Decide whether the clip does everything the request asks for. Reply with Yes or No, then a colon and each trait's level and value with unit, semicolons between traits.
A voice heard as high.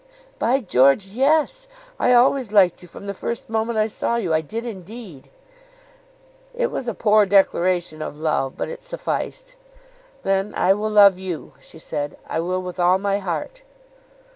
Yes: high, 200 Hz